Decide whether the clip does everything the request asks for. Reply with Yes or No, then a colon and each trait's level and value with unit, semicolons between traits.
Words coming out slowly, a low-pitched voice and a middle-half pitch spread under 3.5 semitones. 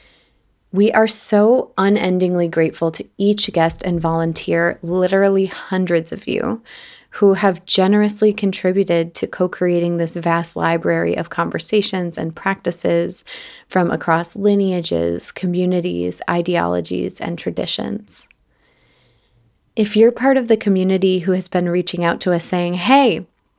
No: slow, 125 wpm; medium, 180 Hz; average, 3.1 semitones